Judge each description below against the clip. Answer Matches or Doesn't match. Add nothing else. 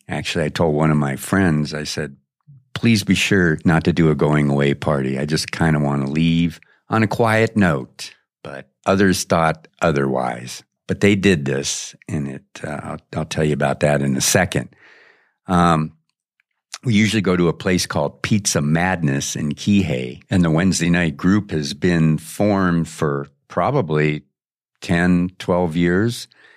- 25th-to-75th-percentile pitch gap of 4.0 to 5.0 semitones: Matches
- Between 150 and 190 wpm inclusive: Matches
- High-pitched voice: Doesn't match